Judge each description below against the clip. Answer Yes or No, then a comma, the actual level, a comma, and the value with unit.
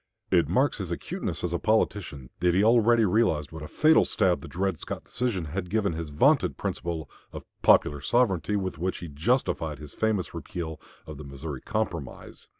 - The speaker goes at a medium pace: Yes, average, 180 wpm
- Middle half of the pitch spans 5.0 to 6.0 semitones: Yes, average, 5.3 semitones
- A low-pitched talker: Yes, very low, 90 Hz